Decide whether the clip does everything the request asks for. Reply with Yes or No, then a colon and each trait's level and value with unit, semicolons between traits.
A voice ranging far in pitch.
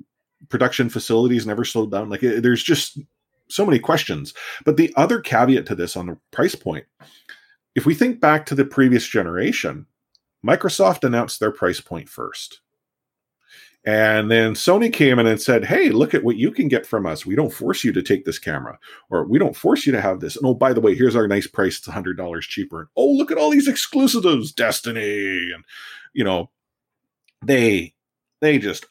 Yes: wide, 5.9 semitones